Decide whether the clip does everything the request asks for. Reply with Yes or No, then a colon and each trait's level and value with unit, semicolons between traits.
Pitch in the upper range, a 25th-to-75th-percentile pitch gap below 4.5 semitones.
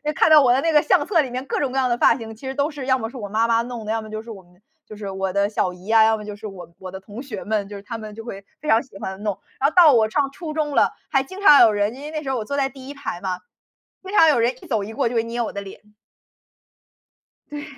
No: high, 230 Hz; average, 4.9 semitones